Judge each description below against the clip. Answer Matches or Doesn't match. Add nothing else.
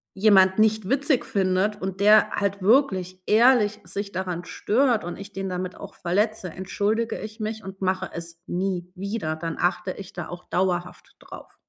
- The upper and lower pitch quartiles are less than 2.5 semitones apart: Doesn't match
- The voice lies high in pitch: Matches